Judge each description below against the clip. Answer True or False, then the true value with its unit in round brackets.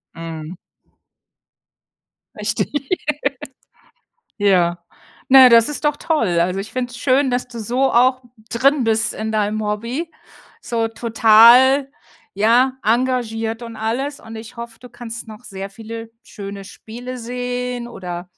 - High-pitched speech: True (230 Hz)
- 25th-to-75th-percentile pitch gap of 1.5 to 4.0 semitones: True (2.6 semitones)